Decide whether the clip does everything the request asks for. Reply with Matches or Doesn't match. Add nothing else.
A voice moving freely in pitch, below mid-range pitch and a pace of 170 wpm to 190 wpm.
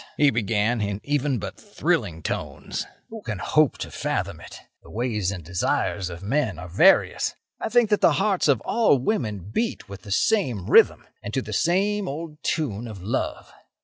Matches